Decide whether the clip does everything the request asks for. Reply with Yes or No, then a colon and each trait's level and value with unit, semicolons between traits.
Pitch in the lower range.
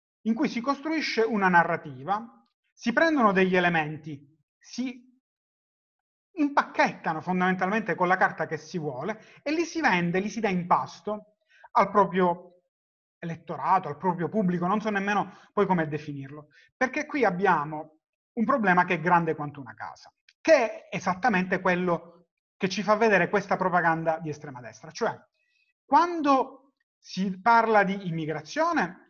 No: high, 195 Hz